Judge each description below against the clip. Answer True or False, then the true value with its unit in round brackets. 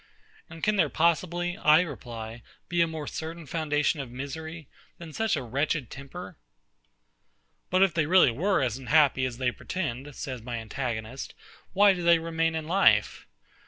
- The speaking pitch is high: False (155 Hz)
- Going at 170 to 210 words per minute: False (160 wpm)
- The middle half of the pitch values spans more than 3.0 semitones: True (4.8 semitones)